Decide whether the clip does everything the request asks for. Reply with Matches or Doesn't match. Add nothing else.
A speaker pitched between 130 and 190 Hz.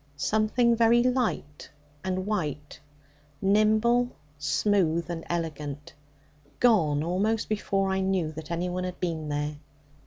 Matches